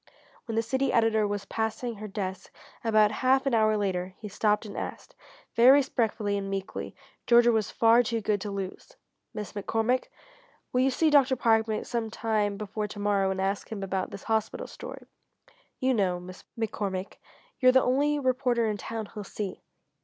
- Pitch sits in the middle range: No, high, 220 Hz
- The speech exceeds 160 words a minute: Yes, average, 175 wpm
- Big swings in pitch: No, average, 2.9 semitones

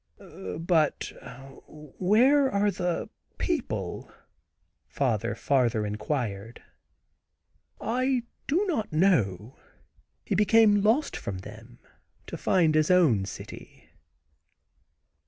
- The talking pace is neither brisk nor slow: No, slow, 90 wpm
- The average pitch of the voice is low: No, medium, 165 Hz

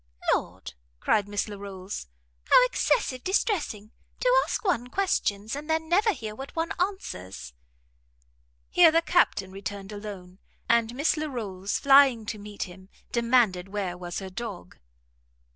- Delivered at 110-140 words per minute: Yes, slow, 135 wpm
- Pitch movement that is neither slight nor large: No, wide, 7.7 semitones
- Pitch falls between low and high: No, high, 220 Hz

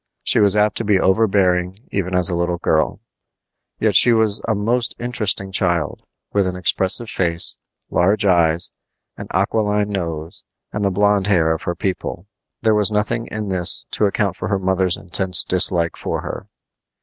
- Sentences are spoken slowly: No, average, 170 wpm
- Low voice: Yes, very low, 95 Hz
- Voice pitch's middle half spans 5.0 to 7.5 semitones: No, average, 2.8 semitones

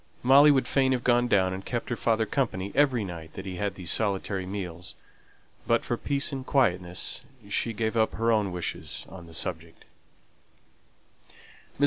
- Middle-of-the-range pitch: No, low, 105 Hz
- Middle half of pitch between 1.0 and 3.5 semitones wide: No, average, 4.8 semitones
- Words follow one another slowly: No, average, 170 wpm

